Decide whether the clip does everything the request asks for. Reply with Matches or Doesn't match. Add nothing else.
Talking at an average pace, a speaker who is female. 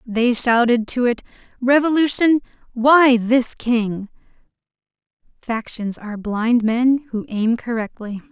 Doesn't match